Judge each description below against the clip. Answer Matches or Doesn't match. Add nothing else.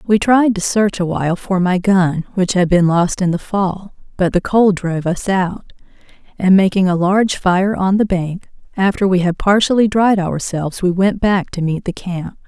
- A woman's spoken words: Matches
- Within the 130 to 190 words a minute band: Doesn't match